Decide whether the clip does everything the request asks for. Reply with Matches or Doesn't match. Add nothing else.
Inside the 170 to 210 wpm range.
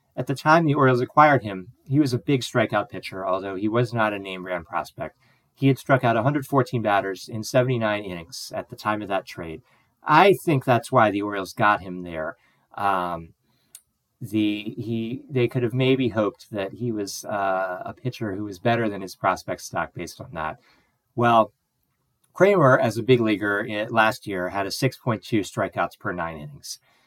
Matches